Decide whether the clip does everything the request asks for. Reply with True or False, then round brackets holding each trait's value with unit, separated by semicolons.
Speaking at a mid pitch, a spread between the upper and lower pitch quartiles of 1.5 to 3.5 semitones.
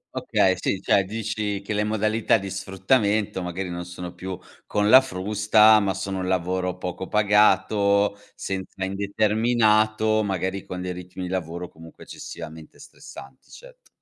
False (100 Hz; 2.6 semitones)